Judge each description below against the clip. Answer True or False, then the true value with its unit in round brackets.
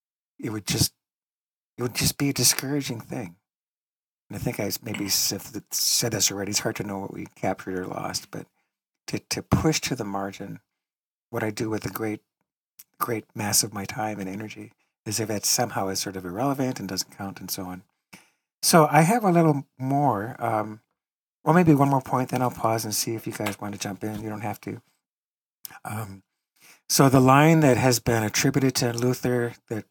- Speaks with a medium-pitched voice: False (115 Hz)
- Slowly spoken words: False (200 wpm)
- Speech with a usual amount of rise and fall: True (4.4 semitones)